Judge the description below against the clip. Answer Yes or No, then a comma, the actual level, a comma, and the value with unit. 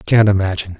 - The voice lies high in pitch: No, low, 100 Hz